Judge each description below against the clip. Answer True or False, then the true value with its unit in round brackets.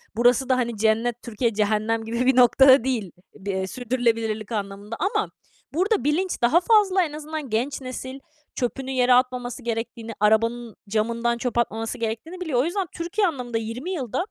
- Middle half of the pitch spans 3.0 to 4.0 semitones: True (3.3 semitones)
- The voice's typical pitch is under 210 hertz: False (245 Hz)